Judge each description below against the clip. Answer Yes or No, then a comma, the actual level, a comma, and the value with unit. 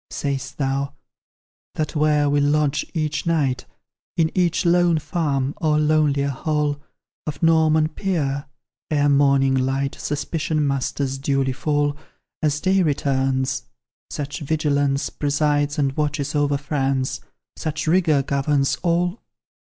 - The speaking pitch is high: No, medium, 145 Hz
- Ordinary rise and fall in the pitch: No, narrow, 2.0 semitones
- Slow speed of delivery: Yes, slow, 120 wpm